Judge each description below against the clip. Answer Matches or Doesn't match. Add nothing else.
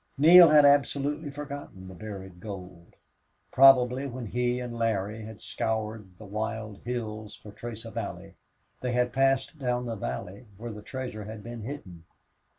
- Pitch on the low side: Matches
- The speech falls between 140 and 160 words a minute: Matches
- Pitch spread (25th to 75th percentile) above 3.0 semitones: Matches